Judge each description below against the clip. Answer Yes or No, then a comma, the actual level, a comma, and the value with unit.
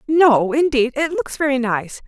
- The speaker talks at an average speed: Yes, average, 175 wpm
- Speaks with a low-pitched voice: No, very high, 260 Hz